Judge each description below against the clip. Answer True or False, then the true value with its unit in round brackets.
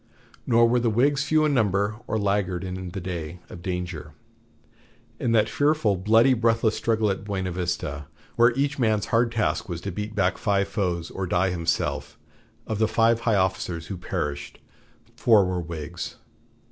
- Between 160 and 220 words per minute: True (170 wpm)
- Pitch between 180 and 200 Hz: False (100 Hz)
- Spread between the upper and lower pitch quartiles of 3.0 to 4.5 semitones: True (4.2 semitones)